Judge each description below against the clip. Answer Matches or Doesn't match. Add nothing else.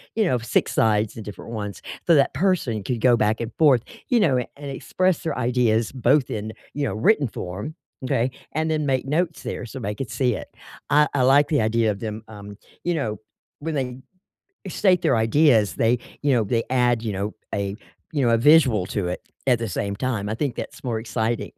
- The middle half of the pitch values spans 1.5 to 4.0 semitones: Doesn't match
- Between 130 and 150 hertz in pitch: Doesn't match